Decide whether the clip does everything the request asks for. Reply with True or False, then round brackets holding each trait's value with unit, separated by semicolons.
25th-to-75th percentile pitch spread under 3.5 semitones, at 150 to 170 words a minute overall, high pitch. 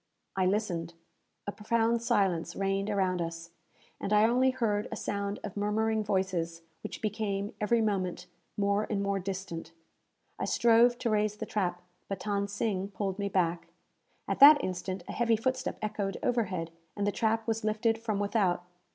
True (2.7 semitones; 165 wpm; 205 Hz)